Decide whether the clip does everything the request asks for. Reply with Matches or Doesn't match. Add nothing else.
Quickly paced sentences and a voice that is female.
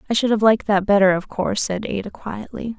Matches